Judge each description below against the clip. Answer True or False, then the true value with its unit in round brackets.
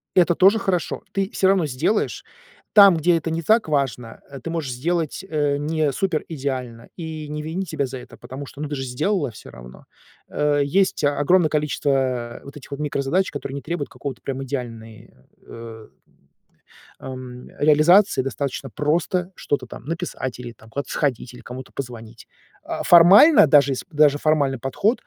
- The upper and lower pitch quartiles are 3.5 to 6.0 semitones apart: True (4.2 semitones)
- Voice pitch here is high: False (145 Hz)